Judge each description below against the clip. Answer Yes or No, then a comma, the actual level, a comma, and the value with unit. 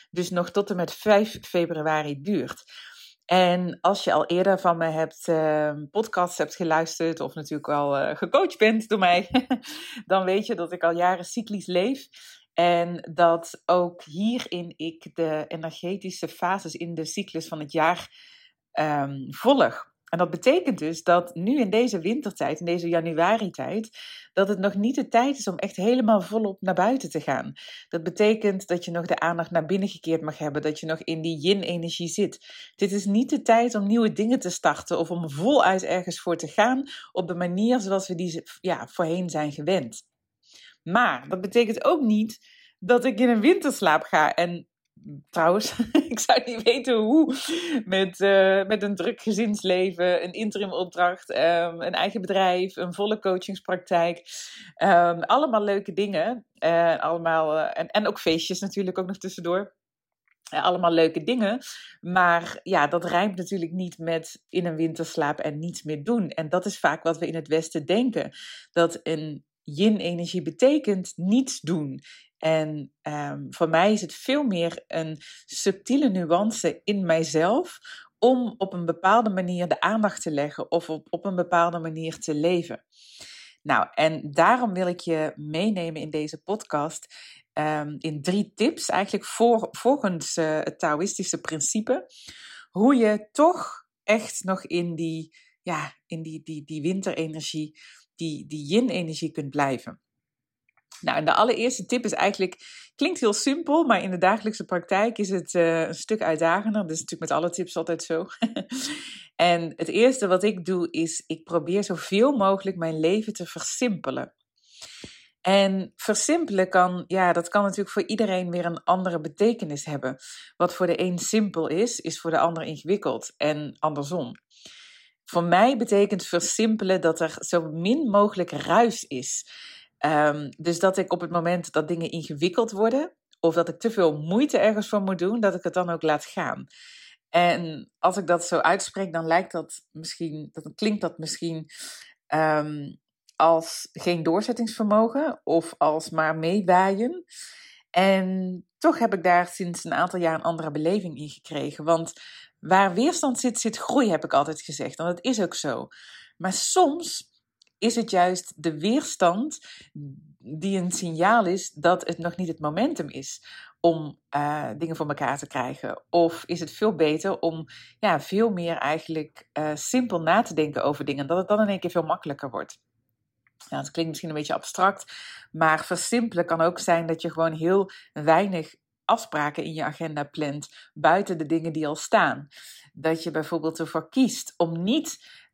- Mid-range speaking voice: Yes, medium, 180 Hz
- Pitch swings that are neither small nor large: Yes, average, 4.5 semitones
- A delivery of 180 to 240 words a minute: No, average, 170 wpm